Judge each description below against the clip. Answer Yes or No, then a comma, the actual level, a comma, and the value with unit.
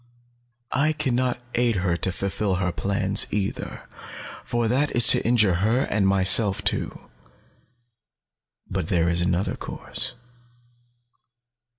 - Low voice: Yes, low, 100 Hz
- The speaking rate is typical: No, slow, 120 wpm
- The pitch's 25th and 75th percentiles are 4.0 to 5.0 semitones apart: Yes, average, 4.4 semitones